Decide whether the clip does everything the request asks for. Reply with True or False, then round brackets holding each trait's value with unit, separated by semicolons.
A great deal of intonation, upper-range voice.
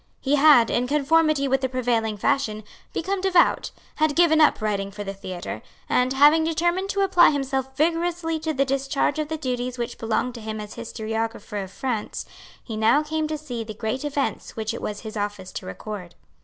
True (6.0 semitones; 260 Hz)